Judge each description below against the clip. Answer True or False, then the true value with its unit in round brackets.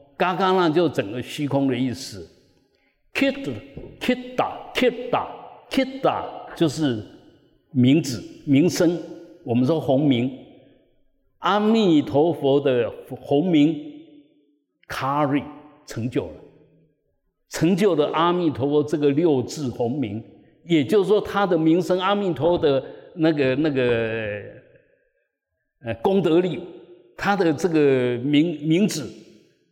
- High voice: False (160 Hz)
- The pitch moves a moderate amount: False (5.7 semitones)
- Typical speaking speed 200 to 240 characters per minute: False (190 characters per minute)